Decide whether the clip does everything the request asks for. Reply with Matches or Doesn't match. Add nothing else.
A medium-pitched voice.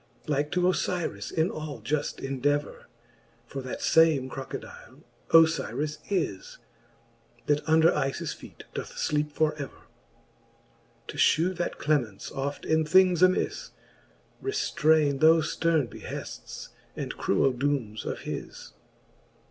Matches